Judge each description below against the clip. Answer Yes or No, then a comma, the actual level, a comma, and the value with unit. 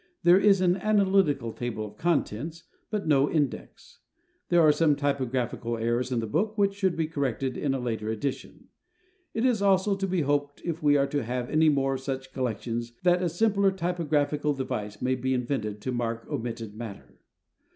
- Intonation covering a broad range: Yes, wide, 6.3 semitones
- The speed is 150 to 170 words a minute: No, average, 180 wpm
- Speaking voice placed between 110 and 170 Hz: Yes, medium, 140 Hz